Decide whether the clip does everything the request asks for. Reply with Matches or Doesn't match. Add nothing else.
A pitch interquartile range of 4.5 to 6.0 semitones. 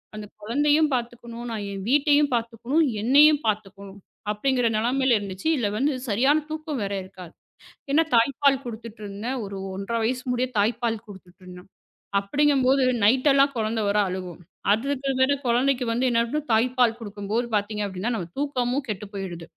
Matches